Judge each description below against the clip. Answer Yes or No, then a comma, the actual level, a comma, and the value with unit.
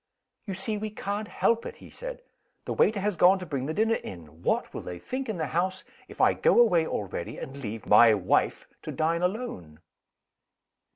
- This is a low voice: No, medium, 180 Hz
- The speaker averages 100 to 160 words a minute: No, average, 195 wpm